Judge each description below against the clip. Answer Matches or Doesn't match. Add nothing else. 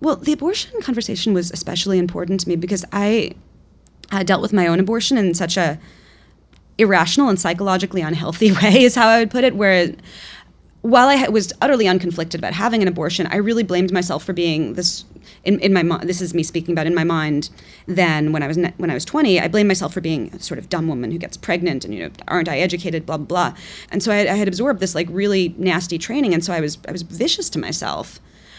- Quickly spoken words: Matches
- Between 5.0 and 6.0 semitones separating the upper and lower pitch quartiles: Doesn't match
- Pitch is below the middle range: Doesn't match